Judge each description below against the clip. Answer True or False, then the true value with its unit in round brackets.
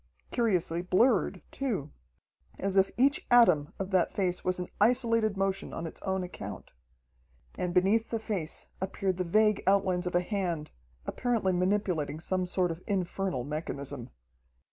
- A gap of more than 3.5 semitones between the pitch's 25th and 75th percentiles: False (3.0 semitones)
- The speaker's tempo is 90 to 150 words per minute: True (145 wpm)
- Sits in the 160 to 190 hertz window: True (185 Hz)